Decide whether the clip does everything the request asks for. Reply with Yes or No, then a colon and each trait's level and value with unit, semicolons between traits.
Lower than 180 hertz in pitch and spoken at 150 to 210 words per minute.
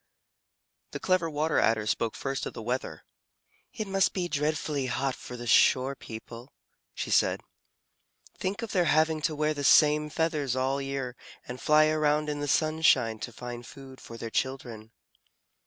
Yes: medium, 140 Hz; average, 170 wpm